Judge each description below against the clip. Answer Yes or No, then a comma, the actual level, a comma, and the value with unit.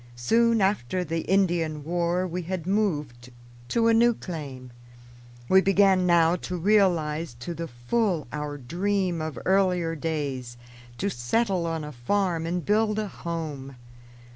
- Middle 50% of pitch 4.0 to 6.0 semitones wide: Yes, average, 4.4 semitones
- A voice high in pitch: No, medium, 170 Hz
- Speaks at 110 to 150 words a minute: Yes, average, 140 wpm